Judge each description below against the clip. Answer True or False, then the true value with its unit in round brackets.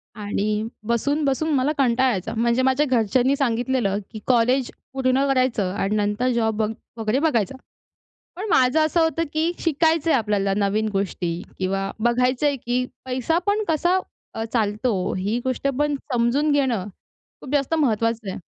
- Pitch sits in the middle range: False (250 Hz)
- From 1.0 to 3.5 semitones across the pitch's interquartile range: False (4.5 semitones)